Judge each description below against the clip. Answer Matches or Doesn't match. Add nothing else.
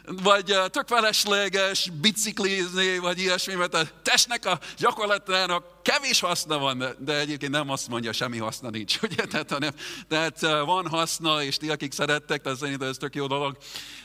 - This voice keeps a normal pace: Doesn't match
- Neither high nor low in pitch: Matches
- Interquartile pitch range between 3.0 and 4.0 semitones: Doesn't match